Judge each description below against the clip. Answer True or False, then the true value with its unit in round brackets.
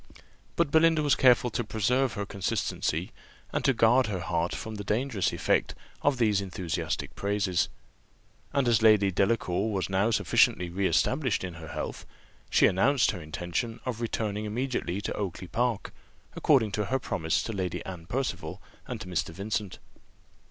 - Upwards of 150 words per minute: True (160 wpm)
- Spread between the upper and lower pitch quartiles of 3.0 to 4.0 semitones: False (4.5 semitones)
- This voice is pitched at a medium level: False (105 Hz)